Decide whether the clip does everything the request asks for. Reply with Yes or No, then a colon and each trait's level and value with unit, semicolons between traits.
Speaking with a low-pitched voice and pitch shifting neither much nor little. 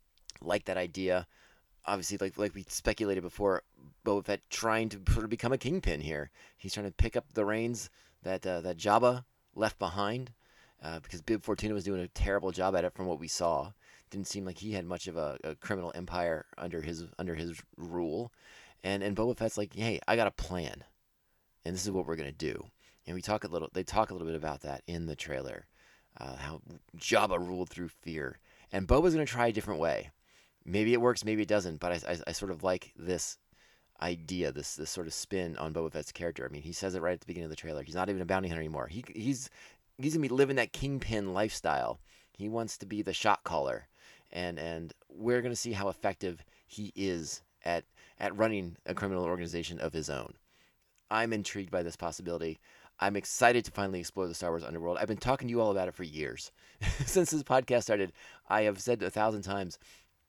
Yes: very low, 95 Hz; average, 4.0 semitones